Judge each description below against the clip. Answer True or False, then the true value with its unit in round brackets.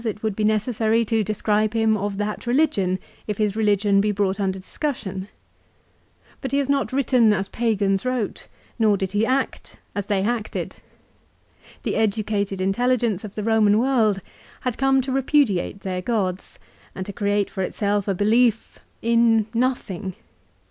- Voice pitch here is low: False (215 Hz)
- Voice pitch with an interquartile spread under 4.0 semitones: True (2.8 semitones)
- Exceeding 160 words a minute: False (155 wpm)